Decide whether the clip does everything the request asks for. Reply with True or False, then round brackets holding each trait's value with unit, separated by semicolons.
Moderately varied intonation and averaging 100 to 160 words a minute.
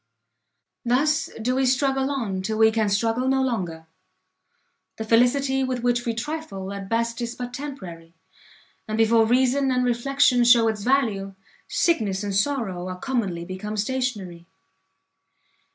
True (4.5 semitones; 140 wpm)